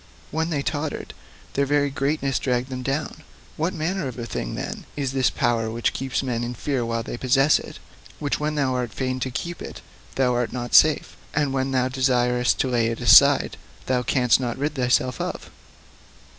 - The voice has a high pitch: No, low, 130 Hz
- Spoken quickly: No, average, 185 wpm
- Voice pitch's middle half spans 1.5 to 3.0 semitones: Yes, narrow, 2.6 semitones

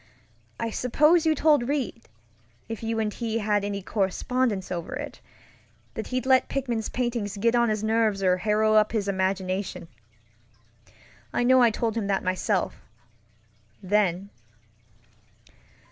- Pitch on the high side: Yes, high, 215 Hz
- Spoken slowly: Yes, slow, 130 wpm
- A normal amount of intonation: Yes, average, 3.8 semitones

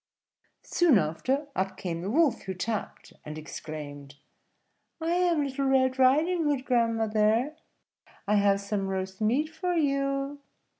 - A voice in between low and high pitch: No, high, 245 Hz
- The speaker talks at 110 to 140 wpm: Yes, slow, 135 wpm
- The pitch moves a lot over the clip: Yes, wide, 6.9 semitones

